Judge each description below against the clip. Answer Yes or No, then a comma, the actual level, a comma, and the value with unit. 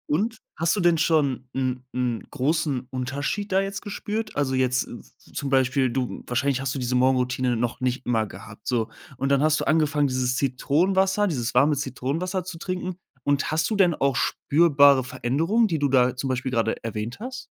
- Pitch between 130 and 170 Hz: Yes, medium, 140 Hz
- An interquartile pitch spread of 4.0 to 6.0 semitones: Yes, average, 4.6 semitones